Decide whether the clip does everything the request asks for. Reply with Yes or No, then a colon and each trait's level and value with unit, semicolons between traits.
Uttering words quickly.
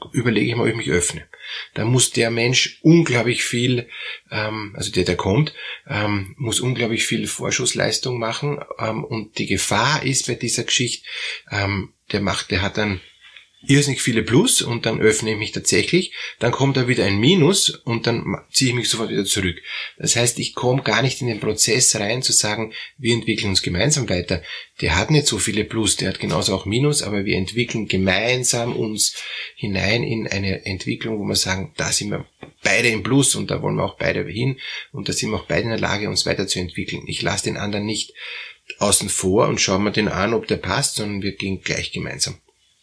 Yes: fast, 200 wpm